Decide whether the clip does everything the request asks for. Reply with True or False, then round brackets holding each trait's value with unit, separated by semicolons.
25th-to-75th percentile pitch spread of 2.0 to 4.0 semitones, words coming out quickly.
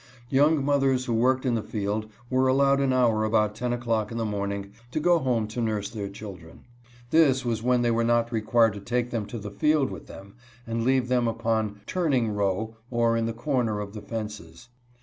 True (3.1 semitones; 210 wpm)